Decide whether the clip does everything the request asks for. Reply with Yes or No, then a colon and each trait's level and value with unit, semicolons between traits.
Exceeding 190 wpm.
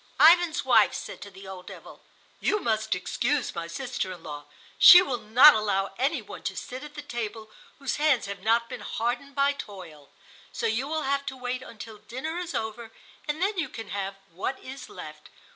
Yes: average, 200 wpm